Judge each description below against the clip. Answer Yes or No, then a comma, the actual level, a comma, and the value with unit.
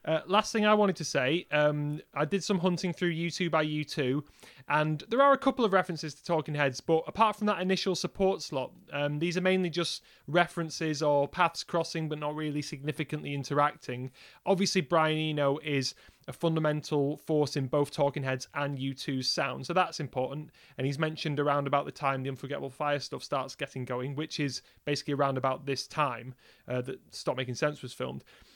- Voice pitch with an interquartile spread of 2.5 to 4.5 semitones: Yes, average, 3.5 semitones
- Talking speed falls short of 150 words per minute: No, average, 195 wpm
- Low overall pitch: No, medium, 150 Hz